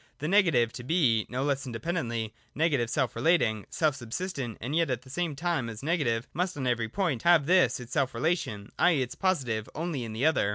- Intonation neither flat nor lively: No, wide, 6.1 semitones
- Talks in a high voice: No, low, 135 Hz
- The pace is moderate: No, fast, 210 wpm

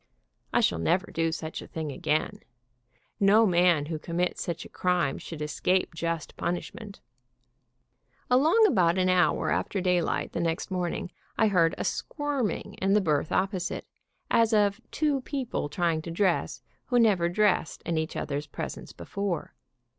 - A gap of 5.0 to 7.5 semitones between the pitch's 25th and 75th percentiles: No, average, 4.0 semitones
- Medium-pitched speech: Yes, medium, 180 Hz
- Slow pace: No, average, 155 wpm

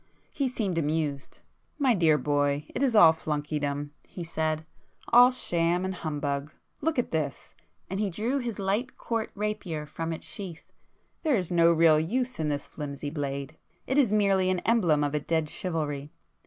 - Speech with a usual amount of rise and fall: No, wide, 6.0 semitones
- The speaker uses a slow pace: No, average, 155 wpm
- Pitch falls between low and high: Yes, medium, 165 Hz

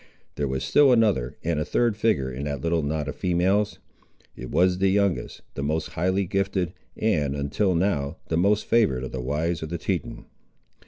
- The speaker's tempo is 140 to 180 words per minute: No, average, 190 wpm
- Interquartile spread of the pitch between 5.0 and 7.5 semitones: Yes, wide, 5.4 semitones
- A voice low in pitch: Yes, very low, 85 Hz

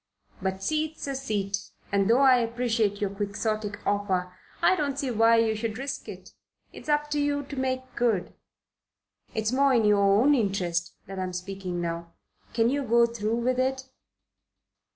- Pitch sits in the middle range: No, high, 225 Hz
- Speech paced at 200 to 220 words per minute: No, average, 175 wpm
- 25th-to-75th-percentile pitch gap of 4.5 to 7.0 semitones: Yes, average, 4.8 semitones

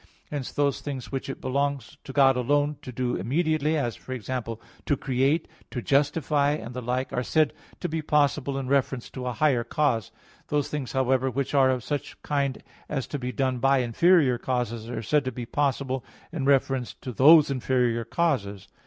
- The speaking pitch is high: No, low, 135 Hz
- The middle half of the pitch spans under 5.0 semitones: Yes, narrow, 2.6 semitones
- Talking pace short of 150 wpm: No, average, 190 wpm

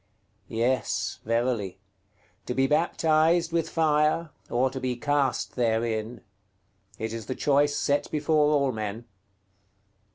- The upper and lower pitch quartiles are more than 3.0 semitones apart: Yes, average, 4.7 semitones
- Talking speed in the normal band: No, slow, 120 wpm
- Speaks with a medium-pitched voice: No, low, 130 Hz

